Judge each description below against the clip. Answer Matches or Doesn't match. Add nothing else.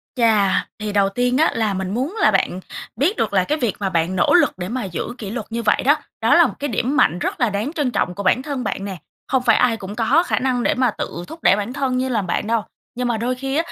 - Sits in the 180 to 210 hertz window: Doesn't match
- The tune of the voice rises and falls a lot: Doesn't match